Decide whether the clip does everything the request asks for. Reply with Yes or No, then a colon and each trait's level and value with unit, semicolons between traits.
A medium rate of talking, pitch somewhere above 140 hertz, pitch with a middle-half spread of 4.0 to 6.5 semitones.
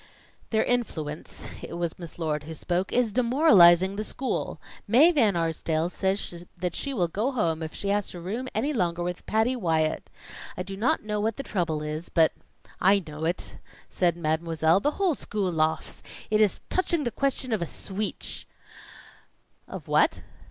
Yes: average, 175 wpm; medium, 185 Hz; wide, 5.4 semitones